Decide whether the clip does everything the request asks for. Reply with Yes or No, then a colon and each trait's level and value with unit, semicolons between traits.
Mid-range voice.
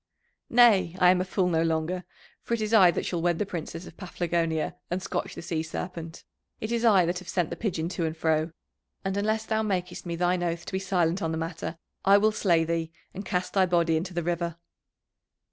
Yes: medium, 175 Hz